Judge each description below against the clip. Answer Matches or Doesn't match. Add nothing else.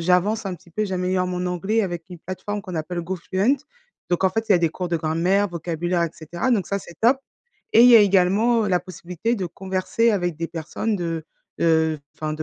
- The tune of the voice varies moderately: Matches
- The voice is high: Doesn't match